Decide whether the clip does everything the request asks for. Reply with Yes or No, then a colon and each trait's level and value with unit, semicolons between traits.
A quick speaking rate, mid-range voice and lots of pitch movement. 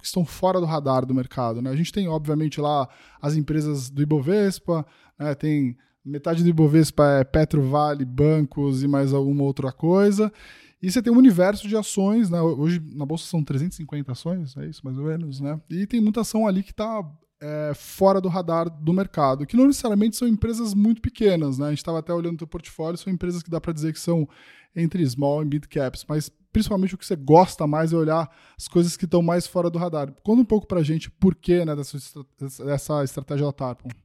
No: fast, 215 wpm; medium, 160 Hz; average, 4.2 semitones